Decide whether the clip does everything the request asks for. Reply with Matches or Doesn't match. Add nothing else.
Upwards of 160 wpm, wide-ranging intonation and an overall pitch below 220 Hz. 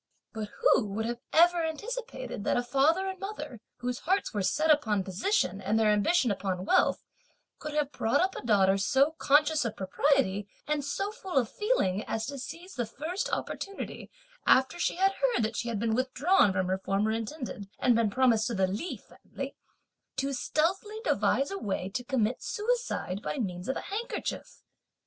Doesn't match